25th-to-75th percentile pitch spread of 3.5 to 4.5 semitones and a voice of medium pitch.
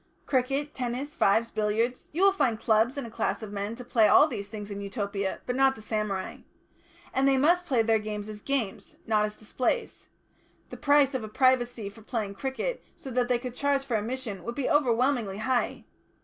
No: average, 3.9 semitones; high, 235 Hz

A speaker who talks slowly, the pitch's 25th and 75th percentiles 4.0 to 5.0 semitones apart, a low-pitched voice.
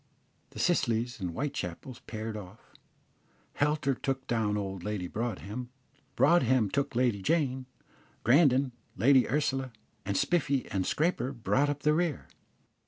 Yes: slow, 125 wpm; average, 4.6 semitones; low, 125 Hz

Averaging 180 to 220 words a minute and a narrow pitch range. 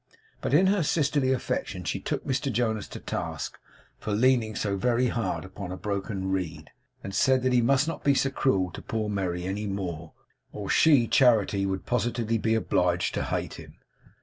No: average, 185 wpm; average, 5.0 semitones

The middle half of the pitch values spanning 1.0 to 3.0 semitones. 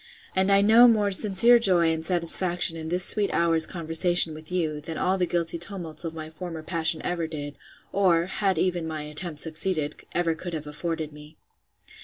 Yes: narrow, 2.6 semitones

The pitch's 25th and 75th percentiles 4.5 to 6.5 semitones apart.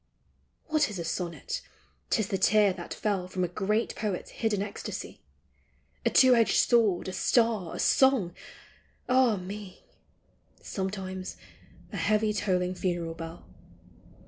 No: average, 3.3 semitones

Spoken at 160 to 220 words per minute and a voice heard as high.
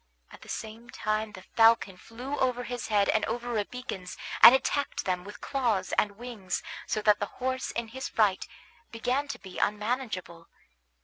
Yes: average, 170 wpm; high, 225 Hz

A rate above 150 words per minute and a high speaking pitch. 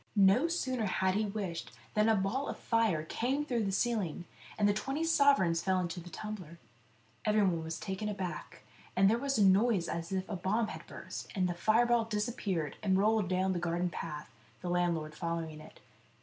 Yes: average, 190 wpm; high, 195 Hz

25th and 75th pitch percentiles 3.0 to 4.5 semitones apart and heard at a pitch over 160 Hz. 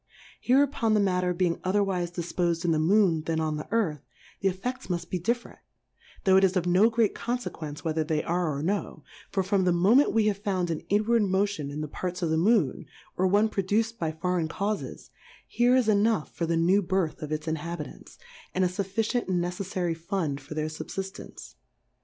Yes: average, 3.7 semitones; medium, 185 Hz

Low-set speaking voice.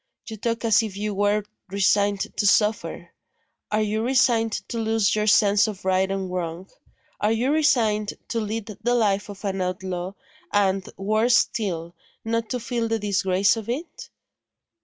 No: high, 210 Hz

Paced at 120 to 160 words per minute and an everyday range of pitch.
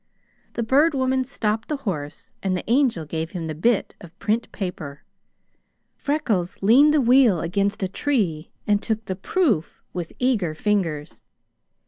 No: average, 150 wpm; wide, 6.8 semitones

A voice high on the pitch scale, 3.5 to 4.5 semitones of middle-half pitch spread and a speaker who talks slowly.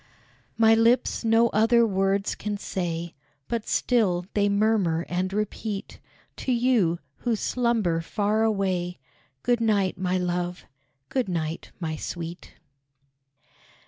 Yes: high, 200 Hz; average, 4.2 semitones; slow, 115 wpm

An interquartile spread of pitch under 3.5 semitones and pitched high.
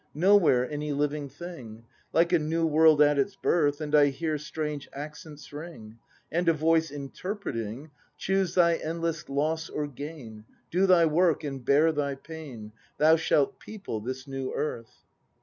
No: average, 2.8 semitones; medium, 150 Hz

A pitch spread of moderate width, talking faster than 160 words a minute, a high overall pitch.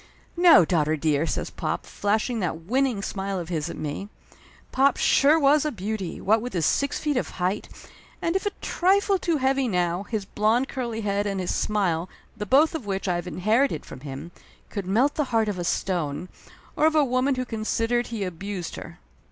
No: wide, 6.6 semitones; average, 200 wpm; high, 210 Hz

